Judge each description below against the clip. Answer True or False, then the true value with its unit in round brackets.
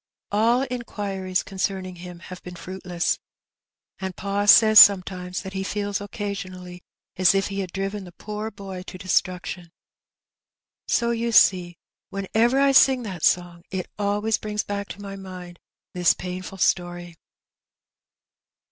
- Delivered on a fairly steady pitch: True (2.2 semitones)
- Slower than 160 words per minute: True (140 wpm)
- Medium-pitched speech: False (195 Hz)